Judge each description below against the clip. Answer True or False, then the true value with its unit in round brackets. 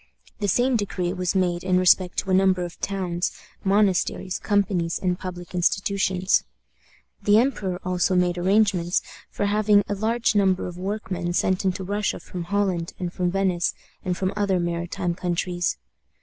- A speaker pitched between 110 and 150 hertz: False (185 Hz)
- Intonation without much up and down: True (2.1 semitones)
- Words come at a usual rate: True (155 wpm)